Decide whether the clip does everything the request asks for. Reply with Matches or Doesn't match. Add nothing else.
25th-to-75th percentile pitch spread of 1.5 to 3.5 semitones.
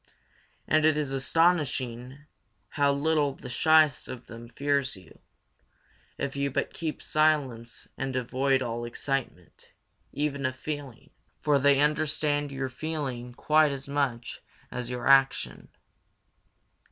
Matches